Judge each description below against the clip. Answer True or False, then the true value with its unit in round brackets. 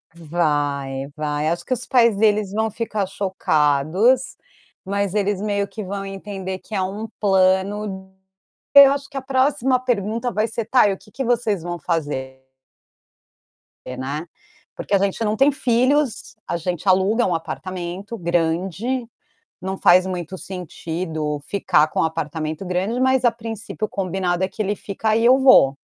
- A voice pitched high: True (195 Hz)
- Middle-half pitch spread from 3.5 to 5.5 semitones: True (4.6 semitones)